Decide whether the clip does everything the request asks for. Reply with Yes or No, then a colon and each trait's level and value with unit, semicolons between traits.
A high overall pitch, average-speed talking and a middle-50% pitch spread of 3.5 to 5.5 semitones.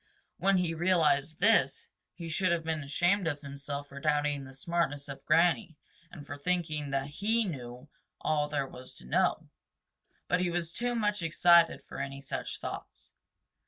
No: medium, 155 Hz; average, 165 wpm; average, 3.8 semitones